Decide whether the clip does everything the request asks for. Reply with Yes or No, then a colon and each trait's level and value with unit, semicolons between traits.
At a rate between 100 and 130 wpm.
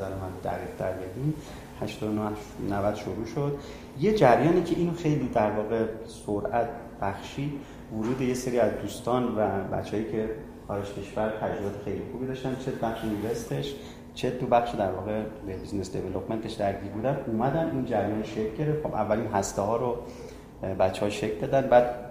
No: fast, 155 wpm